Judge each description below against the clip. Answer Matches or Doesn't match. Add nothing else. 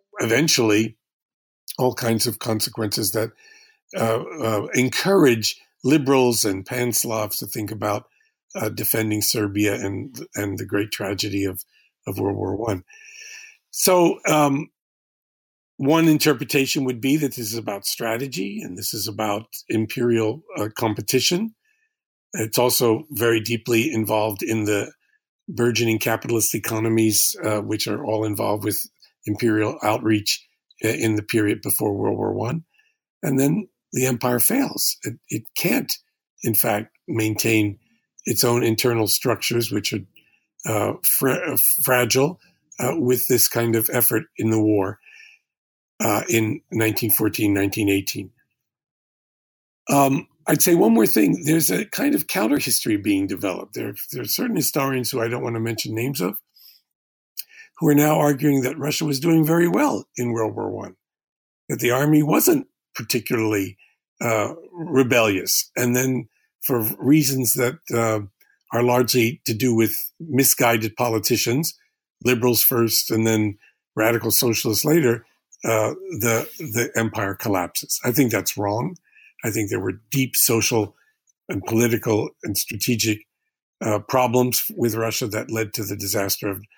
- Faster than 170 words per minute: Doesn't match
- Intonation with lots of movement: Doesn't match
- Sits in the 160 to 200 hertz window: Doesn't match